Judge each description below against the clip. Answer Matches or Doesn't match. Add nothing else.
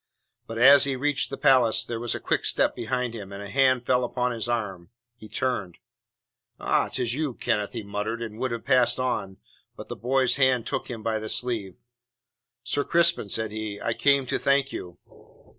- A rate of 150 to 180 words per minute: Doesn't match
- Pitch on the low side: Matches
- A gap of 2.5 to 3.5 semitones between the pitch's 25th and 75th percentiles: Matches